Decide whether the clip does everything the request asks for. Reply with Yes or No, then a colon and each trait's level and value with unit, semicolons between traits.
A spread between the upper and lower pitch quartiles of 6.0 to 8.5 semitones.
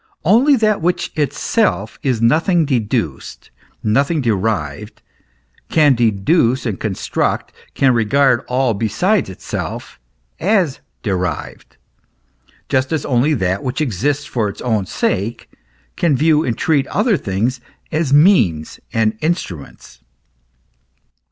Yes: wide, 6.5 semitones